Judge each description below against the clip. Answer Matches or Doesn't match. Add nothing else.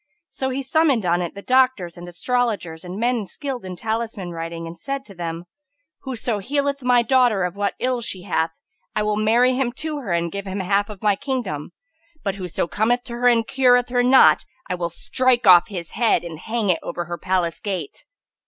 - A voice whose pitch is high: Matches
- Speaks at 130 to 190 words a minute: Doesn't match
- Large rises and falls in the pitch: Matches